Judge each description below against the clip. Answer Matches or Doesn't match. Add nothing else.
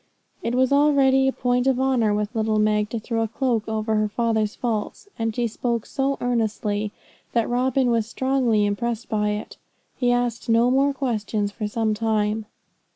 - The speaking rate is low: Doesn't match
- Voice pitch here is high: Matches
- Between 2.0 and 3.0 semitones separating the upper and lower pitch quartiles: Matches